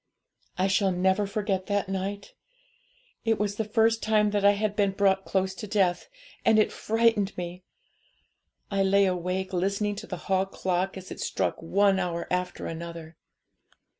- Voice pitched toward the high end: Yes, high, 195 Hz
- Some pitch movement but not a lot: No, narrow, 1.8 semitones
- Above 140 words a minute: Yes, average, 165 wpm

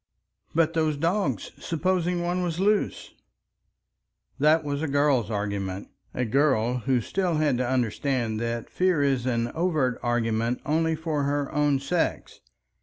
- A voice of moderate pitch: Yes, medium, 145 Hz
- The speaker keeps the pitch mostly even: No, average, 5.2 semitones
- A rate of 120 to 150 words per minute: Yes, average, 140 wpm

